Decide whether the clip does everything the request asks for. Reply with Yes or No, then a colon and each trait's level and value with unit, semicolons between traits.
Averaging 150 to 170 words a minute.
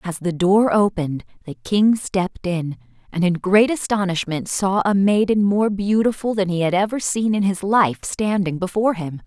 No: average, 180 wpm